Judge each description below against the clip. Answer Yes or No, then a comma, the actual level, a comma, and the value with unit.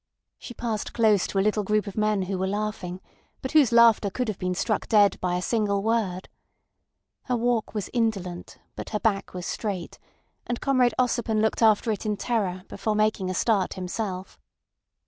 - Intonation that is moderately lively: Yes, average, 3.0 semitones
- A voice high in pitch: Yes, high, 210 Hz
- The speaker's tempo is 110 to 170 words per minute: No, average, 185 wpm